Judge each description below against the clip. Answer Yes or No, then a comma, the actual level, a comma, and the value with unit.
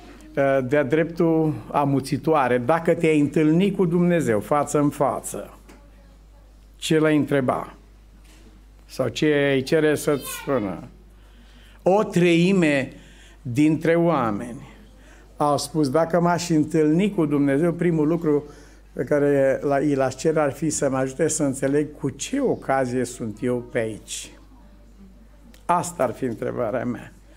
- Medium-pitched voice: Yes, medium, 150 Hz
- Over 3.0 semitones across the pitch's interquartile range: No, average, 2.7 semitones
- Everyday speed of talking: Yes, average, 125 wpm